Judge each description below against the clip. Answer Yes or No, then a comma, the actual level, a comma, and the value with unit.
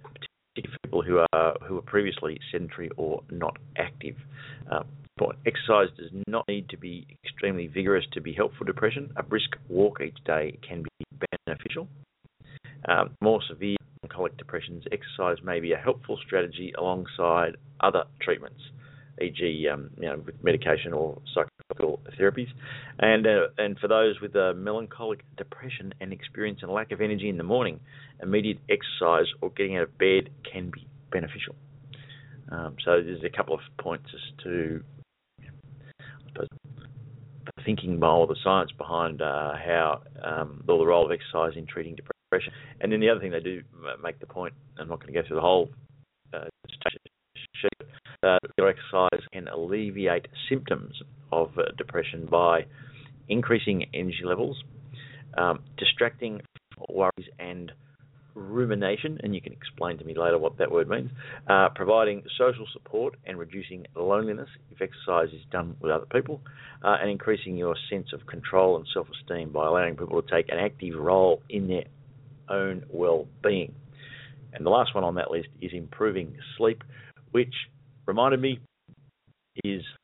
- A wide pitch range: Yes, wide, 5.9 semitones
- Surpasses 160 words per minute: No, average, 155 wpm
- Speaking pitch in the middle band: No, low, 125 Hz